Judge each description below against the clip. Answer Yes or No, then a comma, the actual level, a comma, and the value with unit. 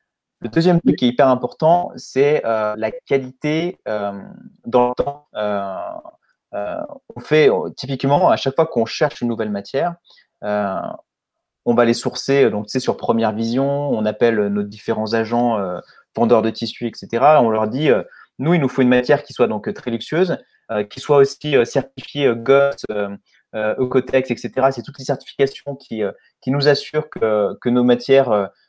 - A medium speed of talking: Yes, average, 190 wpm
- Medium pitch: No, low, 125 Hz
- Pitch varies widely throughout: No, average, 3.8 semitones